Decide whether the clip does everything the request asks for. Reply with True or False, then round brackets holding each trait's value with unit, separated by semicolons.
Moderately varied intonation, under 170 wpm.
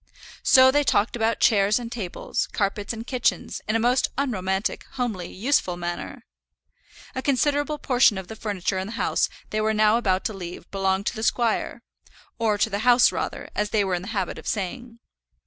False (3.8 semitones; 190 wpm)